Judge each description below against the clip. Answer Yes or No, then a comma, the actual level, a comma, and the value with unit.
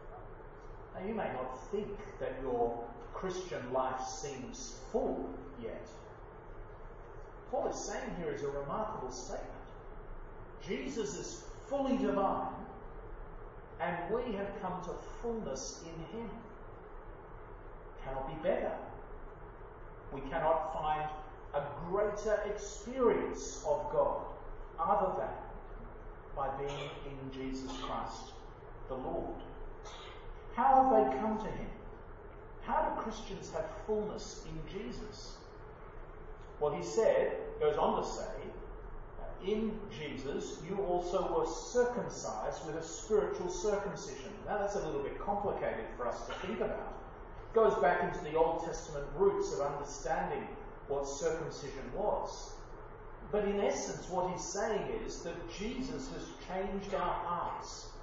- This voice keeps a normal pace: No, slow, 125 wpm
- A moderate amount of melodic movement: No, wide, 5.7 semitones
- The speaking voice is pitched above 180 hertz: Yes, high, 190 Hz